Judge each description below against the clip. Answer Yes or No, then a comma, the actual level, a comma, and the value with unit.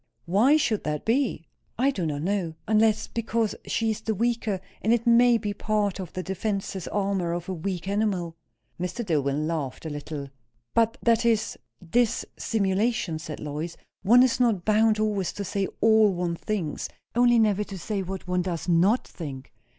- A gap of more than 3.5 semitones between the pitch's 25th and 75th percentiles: Yes, average, 4.4 semitones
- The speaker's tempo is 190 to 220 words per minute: No, average, 175 wpm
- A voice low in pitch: No, high, 200 Hz